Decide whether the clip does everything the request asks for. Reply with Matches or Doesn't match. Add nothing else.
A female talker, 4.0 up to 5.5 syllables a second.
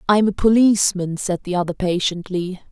Matches